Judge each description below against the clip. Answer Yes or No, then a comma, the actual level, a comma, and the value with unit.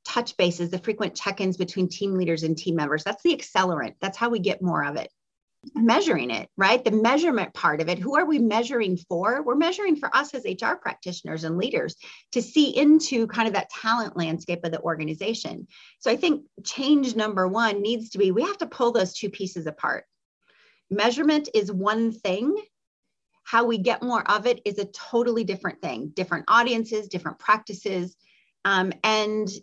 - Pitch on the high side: Yes, high, 215 Hz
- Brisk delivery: No, average, 190 wpm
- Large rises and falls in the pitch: No, average, 4.6 semitones